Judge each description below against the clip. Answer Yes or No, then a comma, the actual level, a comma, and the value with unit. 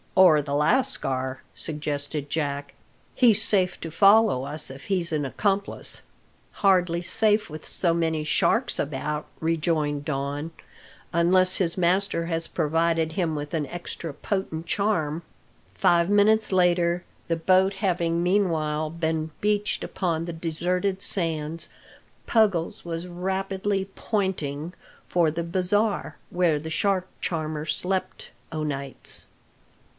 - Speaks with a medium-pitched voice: Yes, medium, 170 Hz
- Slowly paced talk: Yes, slow, 120 wpm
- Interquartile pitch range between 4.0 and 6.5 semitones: No, average, 3.6 semitones